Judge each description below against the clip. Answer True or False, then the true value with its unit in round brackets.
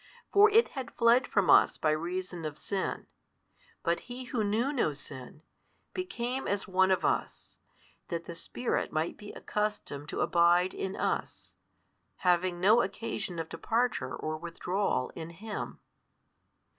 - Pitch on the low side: False (190 Hz)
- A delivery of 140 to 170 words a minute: True (145 wpm)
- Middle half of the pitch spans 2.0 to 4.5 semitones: False (5.5 semitones)